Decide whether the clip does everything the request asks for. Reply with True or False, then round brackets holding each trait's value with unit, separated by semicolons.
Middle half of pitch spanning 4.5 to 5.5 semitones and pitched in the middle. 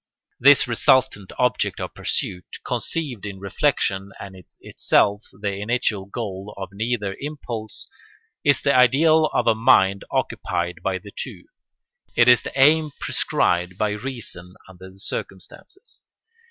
False (5.1 semitones; 105 Hz)